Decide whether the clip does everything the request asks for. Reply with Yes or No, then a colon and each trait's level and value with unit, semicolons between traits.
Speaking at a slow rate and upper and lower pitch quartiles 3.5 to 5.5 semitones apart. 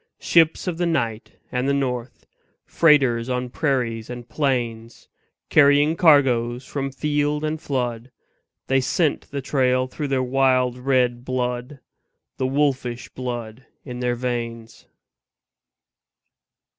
No: slow, 120 wpm; average, 2.7 semitones